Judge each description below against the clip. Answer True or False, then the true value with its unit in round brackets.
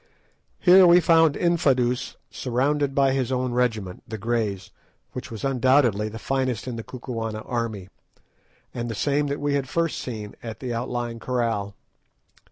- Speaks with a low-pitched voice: True (125 Hz)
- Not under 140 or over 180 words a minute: True (155 wpm)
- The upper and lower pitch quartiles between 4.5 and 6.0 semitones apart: False (3.5 semitones)